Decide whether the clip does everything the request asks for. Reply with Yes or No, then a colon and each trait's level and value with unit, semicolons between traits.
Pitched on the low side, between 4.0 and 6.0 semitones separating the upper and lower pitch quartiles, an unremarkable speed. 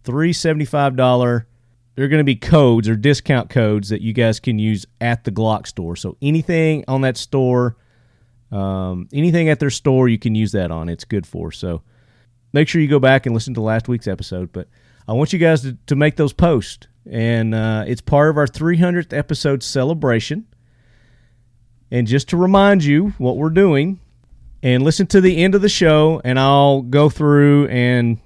Yes: low, 125 Hz; average, 4.4 semitones; average, 190 wpm